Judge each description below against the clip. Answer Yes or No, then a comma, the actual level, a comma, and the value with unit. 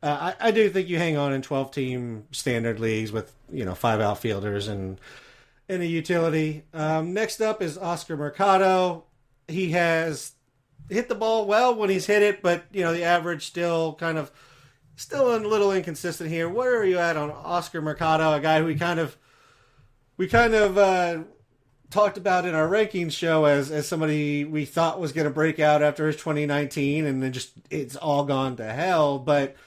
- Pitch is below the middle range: No, medium, 160 Hz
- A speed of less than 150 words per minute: No, average, 190 wpm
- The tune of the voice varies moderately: Yes, average, 4.1 semitones